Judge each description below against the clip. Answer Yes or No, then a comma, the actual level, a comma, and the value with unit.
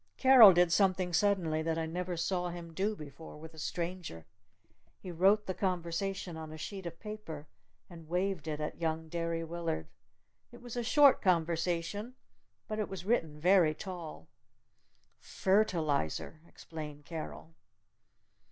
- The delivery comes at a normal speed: Yes, average, 145 wpm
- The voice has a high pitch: No, medium, 170 Hz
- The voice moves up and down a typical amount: Yes, average, 3.2 semitones